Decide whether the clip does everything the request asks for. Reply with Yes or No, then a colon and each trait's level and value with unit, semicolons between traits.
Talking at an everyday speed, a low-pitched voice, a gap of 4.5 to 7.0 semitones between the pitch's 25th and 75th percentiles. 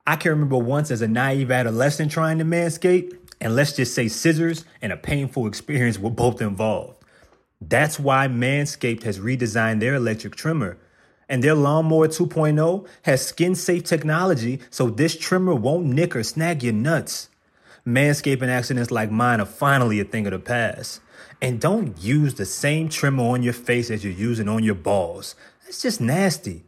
Yes: average, 175 wpm; low, 130 Hz; average, 5.2 semitones